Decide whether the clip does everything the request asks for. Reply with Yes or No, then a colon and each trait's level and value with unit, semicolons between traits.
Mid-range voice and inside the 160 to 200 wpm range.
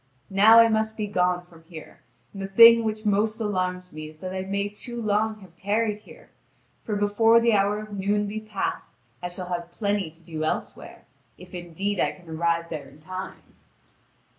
No: high, 200 Hz; average, 190 wpm